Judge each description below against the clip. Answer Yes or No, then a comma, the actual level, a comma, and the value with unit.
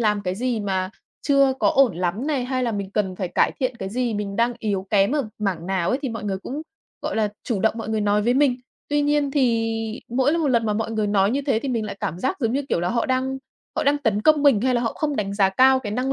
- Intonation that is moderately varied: Yes, average, 4.5 semitones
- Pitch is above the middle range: Yes, high, 230 Hz